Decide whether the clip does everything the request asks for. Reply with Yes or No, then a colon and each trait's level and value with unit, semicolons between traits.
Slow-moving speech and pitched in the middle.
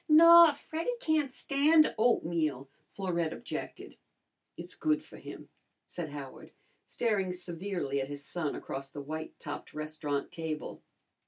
Yes: slow, 130 wpm; medium, 170 Hz